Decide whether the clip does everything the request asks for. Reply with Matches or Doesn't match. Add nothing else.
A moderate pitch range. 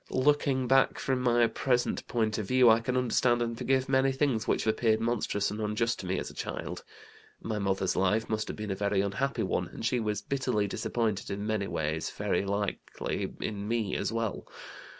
Matches